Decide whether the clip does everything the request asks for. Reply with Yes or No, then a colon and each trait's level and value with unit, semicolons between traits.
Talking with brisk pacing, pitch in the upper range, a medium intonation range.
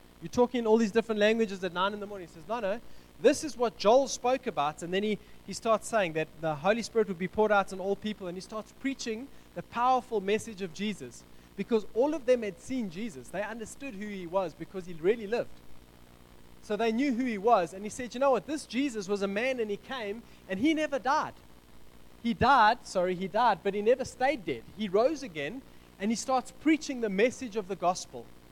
Yes: fast, 230 wpm; high, 215 Hz; average, 4.5 semitones